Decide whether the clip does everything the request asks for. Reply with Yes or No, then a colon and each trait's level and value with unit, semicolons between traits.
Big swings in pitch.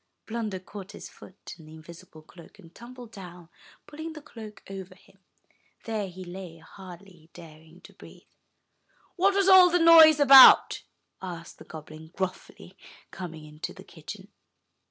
Yes: wide, 6.2 semitones